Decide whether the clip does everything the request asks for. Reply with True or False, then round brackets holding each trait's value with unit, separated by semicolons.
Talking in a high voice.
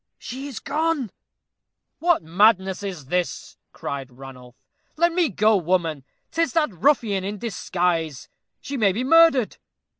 True (200 Hz)